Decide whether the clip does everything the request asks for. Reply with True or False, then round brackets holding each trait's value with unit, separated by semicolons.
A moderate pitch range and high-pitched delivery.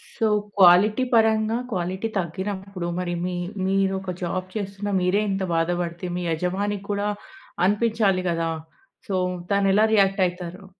False (2.3 semitones; 195 Hz)